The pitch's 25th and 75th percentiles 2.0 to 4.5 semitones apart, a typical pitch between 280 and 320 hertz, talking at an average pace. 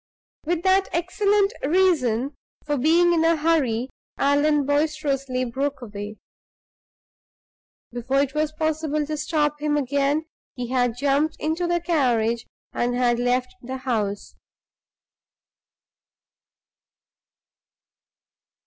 No: average, 4.0 semitones; very high, 285 Hz; slow, 105 wpm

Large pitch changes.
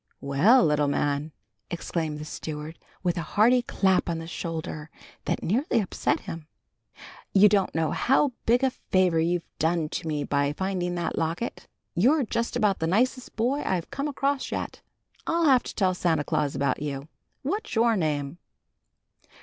Yes: wide, 7.1 semitones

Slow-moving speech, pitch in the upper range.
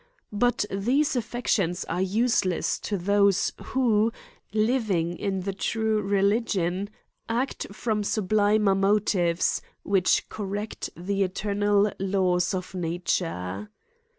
Yes: slow, 105 wpm; high, 200 Hz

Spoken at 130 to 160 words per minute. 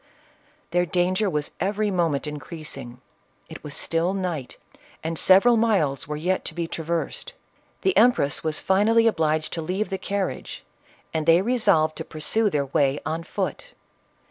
Yes: average, 150 wpm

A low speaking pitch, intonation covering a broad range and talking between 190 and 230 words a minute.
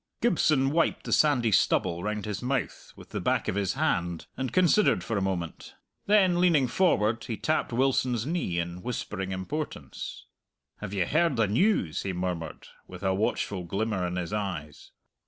No: low, 105 Hz; wide, 7.5 semitones; average, 170 wpm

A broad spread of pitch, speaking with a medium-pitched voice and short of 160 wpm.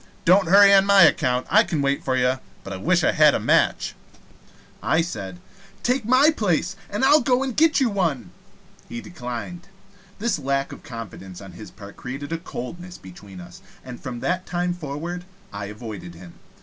No: wide, 8.7 semitones; medium, 150 Hz; average, 185 wpm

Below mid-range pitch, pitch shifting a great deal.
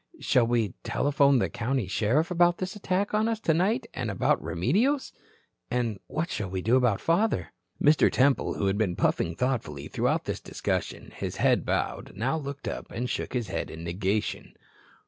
Yes: low, 125 Hz; wide, 8.5 semitones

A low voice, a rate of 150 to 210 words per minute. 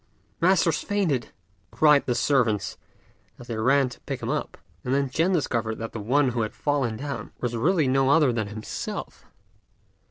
Yes: low, 130 Hz; average, 170 wpm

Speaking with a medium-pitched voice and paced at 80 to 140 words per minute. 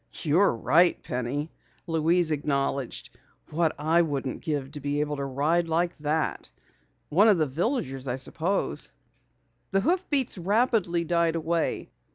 Yes: medium, 160 Hz; slow, 135 wpm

